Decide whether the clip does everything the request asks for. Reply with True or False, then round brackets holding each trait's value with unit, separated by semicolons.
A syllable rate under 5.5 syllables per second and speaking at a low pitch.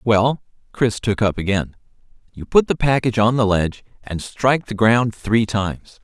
True (4.9 syllables/s; 110 Hz)